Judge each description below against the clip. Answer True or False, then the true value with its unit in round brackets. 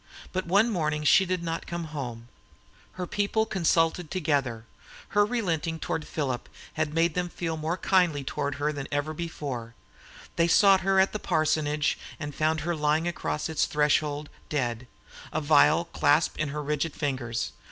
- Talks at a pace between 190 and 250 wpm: False (165 wpm)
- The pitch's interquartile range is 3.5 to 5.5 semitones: False (2.8 semitones)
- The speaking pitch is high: False (155 Hz)